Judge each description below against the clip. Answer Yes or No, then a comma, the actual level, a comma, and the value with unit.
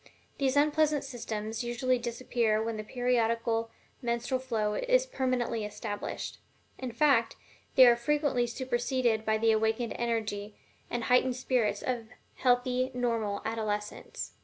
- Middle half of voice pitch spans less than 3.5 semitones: Yes, narrow, 2.5 semitones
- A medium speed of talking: No, slow, 125 wpm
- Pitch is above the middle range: Yes, high, 240 Hz